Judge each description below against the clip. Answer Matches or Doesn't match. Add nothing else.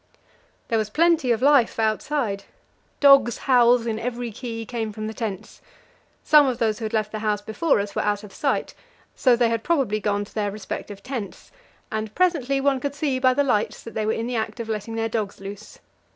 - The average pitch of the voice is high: Matches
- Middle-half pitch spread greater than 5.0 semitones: Doesn't match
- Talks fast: Matches